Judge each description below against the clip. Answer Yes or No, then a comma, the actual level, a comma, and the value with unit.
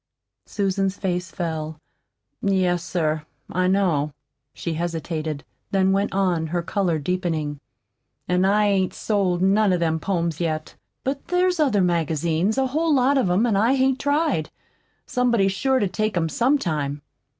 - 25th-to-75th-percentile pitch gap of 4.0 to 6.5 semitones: Yes, average, 4.5 semitones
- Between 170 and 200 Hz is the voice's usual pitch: Yes, medium, 185 Hz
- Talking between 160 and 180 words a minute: No, average, 150 wpm